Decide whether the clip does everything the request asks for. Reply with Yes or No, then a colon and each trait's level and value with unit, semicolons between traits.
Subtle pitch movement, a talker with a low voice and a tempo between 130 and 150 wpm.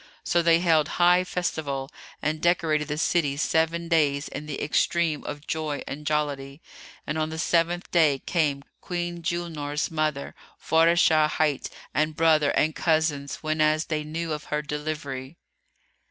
No: narrow, 2.0 semitones; medium, 155 Hz; average, 145 wpm